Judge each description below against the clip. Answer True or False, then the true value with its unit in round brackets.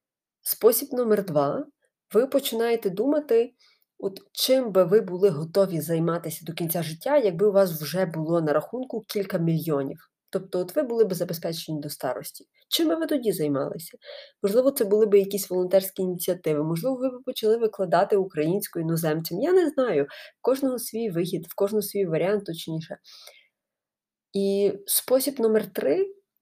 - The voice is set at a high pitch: True (200 Hz)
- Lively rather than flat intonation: True (6.5 semitones)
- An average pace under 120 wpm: False (155 wpm)